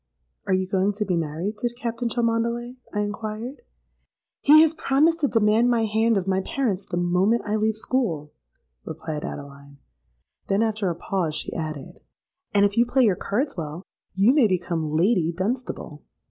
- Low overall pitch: No, high, 210 Hz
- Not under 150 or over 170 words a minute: Yes, average, 165 wpm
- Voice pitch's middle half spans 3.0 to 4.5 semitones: No, average, 5.1 semitones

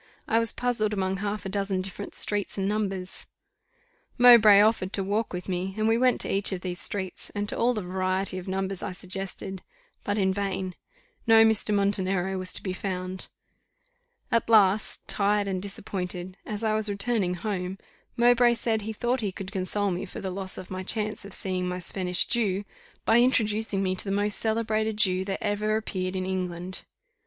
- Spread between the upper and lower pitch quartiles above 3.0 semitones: No, narrow, 2.4 semitones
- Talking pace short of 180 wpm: No, average, 190 wpm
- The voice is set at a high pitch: Yes, high, 195 Hz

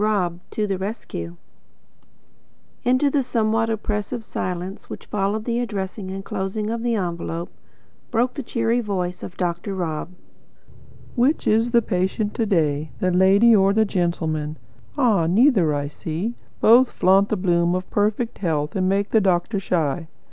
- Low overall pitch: No, high, 195 Hz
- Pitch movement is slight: No, average, 4.1 semitones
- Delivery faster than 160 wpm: No, average, 155 wpm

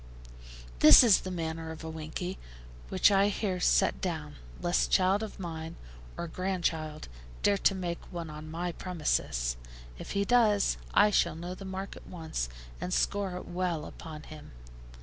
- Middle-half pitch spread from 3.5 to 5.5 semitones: No, average, 3.1 semitones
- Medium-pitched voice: Yes, medium, 175 Hz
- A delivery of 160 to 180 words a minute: Yes, average, 165 wpm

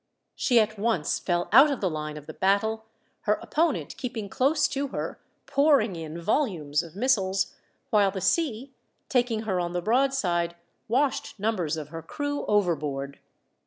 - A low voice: No, high, 205 Hz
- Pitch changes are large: Yes, wide, 7.0 semitones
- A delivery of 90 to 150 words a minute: No, average, 165 wpm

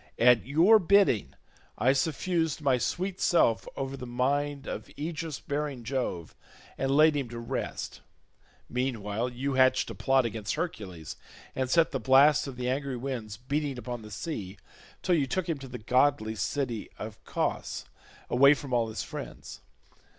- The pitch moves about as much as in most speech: Yes, average, 3.4 semitones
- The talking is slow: No, average, 160 wpm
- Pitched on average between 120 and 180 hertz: Yes, low, 135 Hz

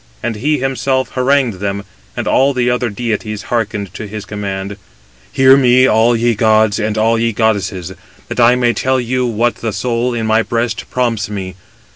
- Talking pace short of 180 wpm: No, average, 185 wpm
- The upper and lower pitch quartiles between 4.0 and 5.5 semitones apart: No, average, 2.8 semitones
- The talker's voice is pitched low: Yes, low, 115 Hz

